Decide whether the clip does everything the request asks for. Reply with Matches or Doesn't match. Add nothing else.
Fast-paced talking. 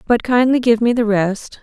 Matches